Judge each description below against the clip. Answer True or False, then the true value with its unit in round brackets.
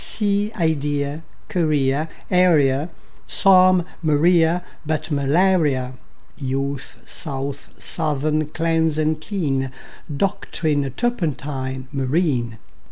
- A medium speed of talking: False (80 wpm)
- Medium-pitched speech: True (155 Hz)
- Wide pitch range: False (3.8 semitones)